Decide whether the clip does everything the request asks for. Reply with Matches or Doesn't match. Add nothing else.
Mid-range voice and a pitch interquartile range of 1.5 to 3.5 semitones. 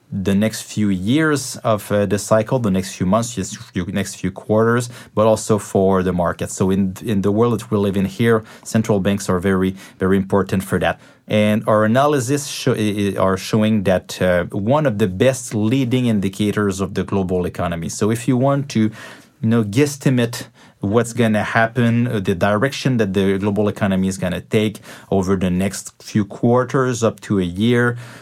Doesn't match